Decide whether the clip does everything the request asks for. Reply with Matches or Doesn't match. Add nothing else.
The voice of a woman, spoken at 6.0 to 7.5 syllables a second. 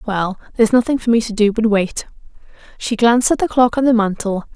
Matches